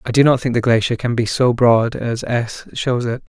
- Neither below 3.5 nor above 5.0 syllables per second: Yes, 4.8 syllables/s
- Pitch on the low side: Yes, low, 120 Hz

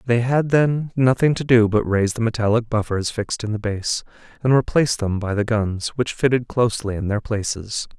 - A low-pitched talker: Yes, low, 115 Hz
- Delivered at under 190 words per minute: No, fast, 205 wpm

